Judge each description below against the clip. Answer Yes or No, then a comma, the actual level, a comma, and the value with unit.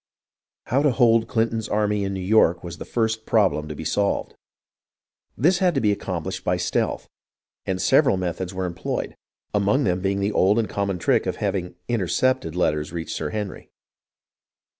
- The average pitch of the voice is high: No, low, 100 Hz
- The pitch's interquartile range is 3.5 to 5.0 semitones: Yes, average, 3.9 semitones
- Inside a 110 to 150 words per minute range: No, average, 170 wpm